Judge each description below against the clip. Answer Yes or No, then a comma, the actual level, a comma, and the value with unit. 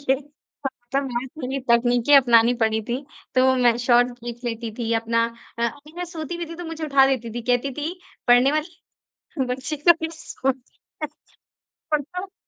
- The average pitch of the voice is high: Yes, very high, 260 Hz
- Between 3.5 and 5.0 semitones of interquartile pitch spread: Yes, average, 4.2 semitones